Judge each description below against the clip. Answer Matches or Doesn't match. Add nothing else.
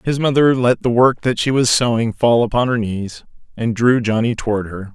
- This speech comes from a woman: Doesn't match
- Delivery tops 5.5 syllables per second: Doesn't match